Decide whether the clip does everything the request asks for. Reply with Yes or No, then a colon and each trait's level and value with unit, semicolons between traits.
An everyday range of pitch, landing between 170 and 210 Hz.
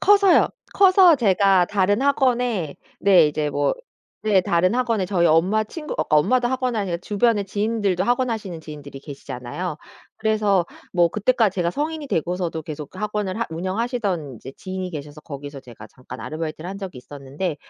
No: wide, 6.2 semitones; medium, 185 Hz